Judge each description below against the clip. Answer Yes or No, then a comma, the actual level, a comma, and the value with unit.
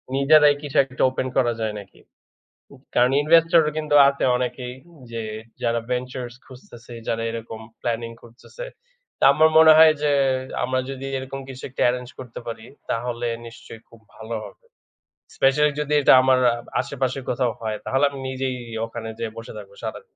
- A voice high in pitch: No, low, 125 Hz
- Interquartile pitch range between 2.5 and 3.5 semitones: Yes, average, 3.0 semitones